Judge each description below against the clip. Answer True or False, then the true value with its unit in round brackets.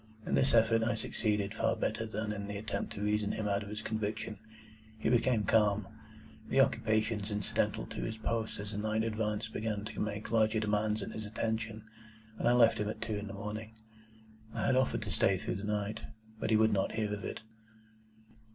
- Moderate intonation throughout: False (1.2 semitones)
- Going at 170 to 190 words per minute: False (205 wpm)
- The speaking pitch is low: True (110 Hz)